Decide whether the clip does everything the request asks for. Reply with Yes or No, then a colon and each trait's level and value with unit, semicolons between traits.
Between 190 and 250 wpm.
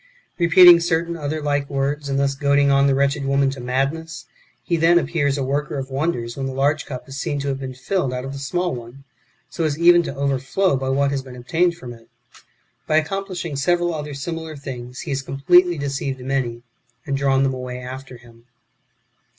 Yes: average, 200 wpm